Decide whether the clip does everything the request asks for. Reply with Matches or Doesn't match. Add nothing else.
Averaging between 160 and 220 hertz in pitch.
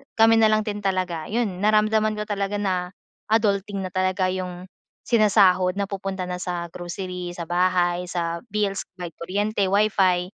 Matches